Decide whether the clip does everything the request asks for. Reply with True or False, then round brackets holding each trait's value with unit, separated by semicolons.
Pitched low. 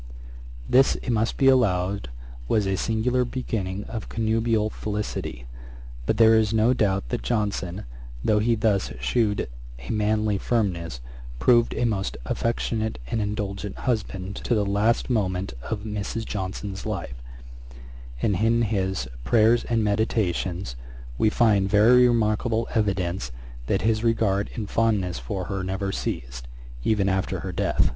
True (105 Hz)